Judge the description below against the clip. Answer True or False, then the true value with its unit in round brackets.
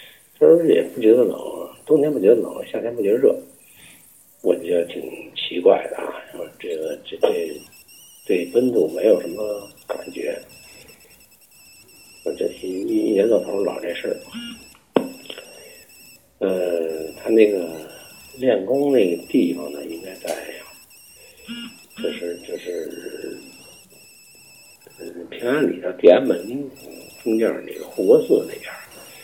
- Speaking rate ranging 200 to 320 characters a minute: False (180 characters per minute)